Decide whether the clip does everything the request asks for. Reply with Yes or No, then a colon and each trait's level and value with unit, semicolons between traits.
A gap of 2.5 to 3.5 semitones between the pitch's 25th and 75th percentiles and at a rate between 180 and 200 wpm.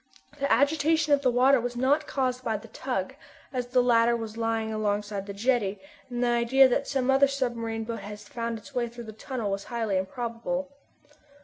Yes: average, 3.0 semitones; average, 195 wpm